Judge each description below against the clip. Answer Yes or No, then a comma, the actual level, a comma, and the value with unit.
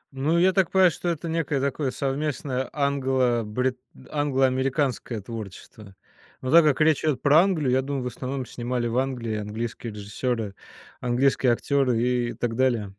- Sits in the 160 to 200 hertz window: No, low, 130 Hz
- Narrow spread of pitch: No, average, 3.2 semitones